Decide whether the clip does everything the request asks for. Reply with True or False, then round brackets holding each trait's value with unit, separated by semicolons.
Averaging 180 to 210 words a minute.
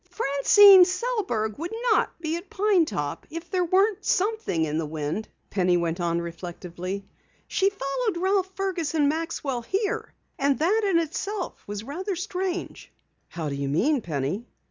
False (145 wpm)